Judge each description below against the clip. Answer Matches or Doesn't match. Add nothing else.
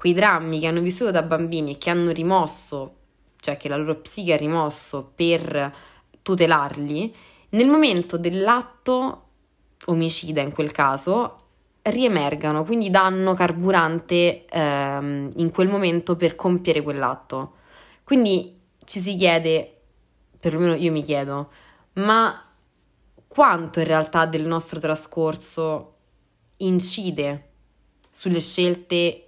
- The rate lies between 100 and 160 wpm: Matches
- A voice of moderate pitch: Matches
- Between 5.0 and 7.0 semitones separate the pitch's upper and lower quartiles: Doesn't match